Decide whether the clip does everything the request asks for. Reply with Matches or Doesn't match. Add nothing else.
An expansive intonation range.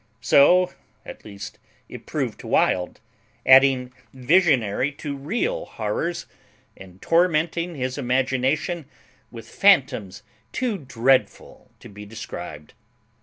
Matches